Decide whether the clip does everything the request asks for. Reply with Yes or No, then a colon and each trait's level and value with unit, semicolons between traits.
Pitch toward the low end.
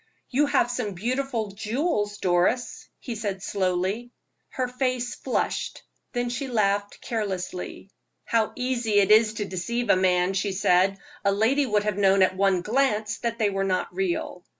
No: high, 210 Hz